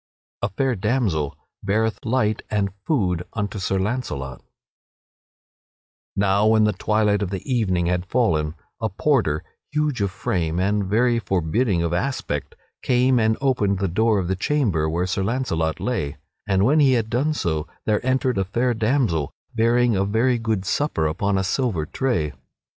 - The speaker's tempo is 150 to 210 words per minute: Yes, average, 165 wpm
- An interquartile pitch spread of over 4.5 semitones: Yes, average, 5.2 semitones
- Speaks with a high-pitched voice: No, low, 105 Hz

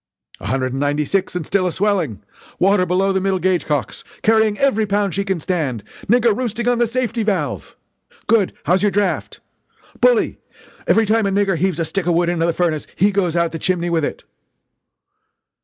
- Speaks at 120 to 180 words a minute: No, average, 195 wpm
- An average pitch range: Yes, average, 3.7 semitones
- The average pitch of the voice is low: No, high, 190 Hz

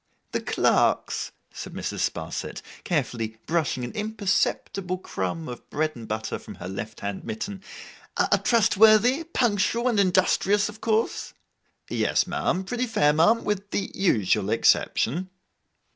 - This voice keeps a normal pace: No, slow, 130 wpm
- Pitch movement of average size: No, wide, 8.0 semitones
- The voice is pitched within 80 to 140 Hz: No, high, 190 Hz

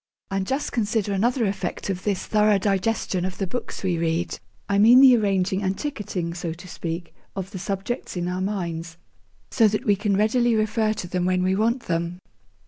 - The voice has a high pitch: Yes, high, 195 Hz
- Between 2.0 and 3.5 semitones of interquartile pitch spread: Yes, average, 3.1 semitones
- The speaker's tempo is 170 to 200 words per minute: Yes, average, 195 wpm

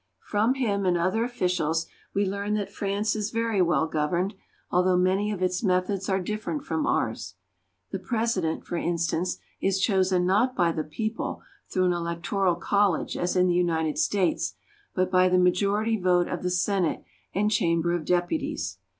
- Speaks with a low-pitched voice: No, medium, 185 Hz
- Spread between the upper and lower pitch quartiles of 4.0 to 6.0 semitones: No, average, 2.7 semitones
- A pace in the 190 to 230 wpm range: No, average, 170 wpm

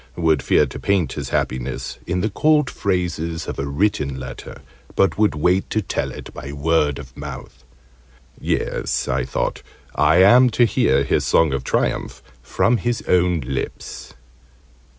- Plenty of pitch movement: Yes, wide, 6.2 semitones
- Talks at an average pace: Yes, average, 155 wpm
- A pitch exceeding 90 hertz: No, very low, 80 Hz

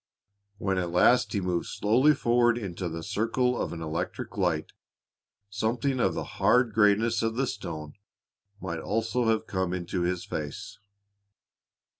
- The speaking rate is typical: Yes, average, 145 wpm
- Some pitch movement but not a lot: Yes, average, 4.9 semitones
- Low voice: Yes, low, 100 Hz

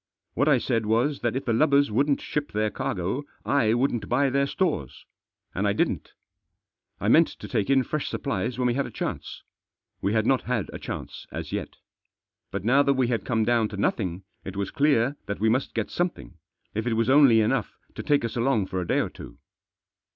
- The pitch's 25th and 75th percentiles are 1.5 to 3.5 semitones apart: No, average, 4.2 semitones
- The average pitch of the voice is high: No, low, 120 Hz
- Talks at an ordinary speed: No, fast, 215 wpm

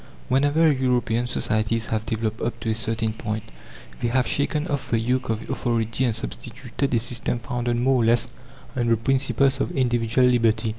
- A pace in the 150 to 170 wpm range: No, average, 180 wpm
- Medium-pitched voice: No, low, 120 Hz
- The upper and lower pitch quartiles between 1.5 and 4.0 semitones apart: Yes, narrow, 2.4 semitones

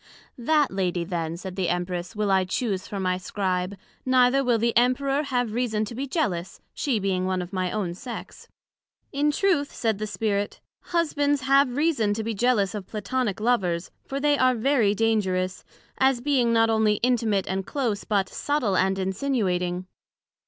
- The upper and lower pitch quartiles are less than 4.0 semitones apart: No, average, 5.2 semitones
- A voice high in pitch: Yes, high, 215 Hz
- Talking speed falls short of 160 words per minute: No, average, 170 wpm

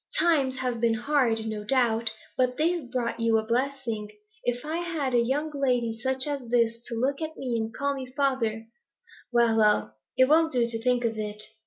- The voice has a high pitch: Yes, high, 245 Hz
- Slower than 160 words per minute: No, average, 195 wpm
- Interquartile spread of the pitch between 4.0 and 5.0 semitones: No, average, 3.3 semitones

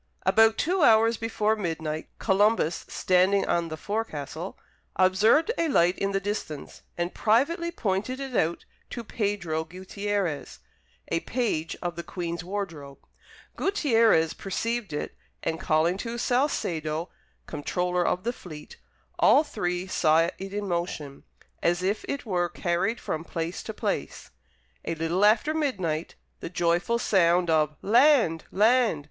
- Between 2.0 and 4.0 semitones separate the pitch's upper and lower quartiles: No, average, 5.1 semitones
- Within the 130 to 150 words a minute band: Yes, slow, 135 wpm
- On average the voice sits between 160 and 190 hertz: Yes, medium, 185 Hz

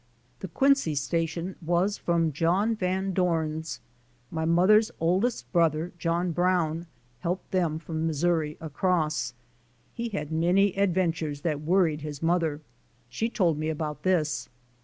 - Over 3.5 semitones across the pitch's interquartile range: No, average, 2.9 semitones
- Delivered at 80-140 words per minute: Yes, slow, 135 wpm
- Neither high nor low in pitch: Yes, medium, 170 Hz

